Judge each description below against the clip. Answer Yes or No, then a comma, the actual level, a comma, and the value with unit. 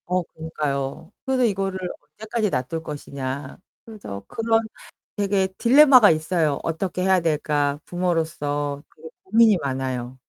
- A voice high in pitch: No, medium, 165 Hz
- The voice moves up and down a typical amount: No, wide, 5.7 semitones